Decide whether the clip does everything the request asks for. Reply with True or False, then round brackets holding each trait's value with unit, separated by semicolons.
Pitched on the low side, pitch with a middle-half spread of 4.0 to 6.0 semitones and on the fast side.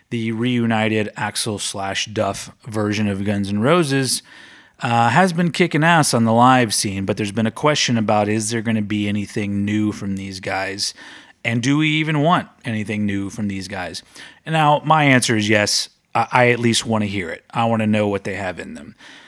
False (110 Hz; 3.5 semitones; 210 wpm)